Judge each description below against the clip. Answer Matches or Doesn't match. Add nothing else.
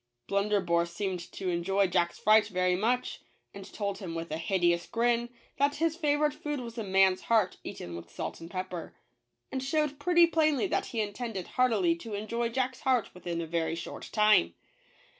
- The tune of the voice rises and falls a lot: Matches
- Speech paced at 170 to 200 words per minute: Matches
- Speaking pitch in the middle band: Doesn't match